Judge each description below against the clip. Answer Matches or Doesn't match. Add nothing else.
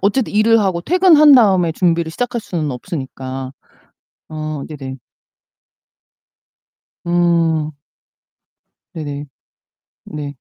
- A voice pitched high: Doesn't match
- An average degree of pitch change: Doesn't match